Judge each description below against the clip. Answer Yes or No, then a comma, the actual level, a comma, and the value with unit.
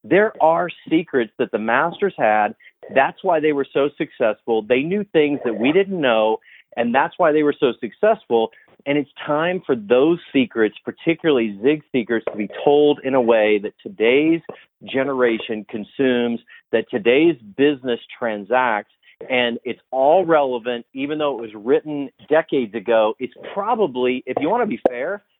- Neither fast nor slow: Yes, average, 165 wpm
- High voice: No, low, 135 Hz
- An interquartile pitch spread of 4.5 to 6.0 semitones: Yes, average, 5.0 semitones